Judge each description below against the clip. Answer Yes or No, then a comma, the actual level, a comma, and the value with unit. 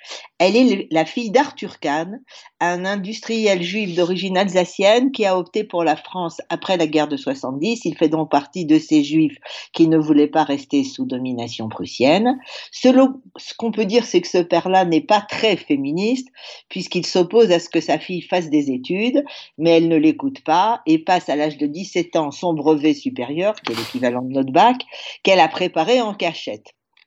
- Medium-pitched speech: Yes, medium, 180 Hz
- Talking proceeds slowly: No, average, 190 wpm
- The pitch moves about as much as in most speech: No, wide, 6.5 semitones